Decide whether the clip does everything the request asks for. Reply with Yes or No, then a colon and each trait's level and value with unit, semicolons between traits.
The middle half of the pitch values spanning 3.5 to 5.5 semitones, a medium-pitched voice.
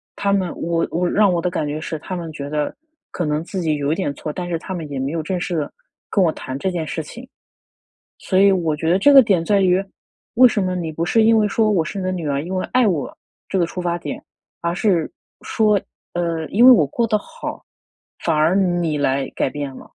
Yes: average, 3.9 semitones; medium, 175 Hz